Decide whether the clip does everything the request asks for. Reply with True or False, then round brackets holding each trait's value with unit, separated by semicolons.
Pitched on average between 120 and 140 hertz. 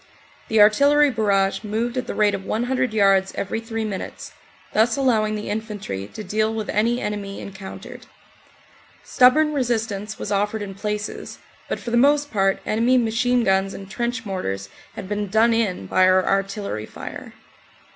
False (215 Hz)